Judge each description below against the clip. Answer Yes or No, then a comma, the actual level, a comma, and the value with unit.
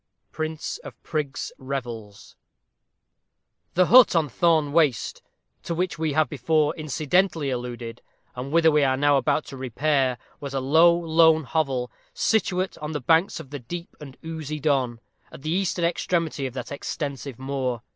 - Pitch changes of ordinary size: Yes, average, 3.5 semitones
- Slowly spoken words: No, average, 155 wpm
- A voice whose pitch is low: No, medium, 150 Hz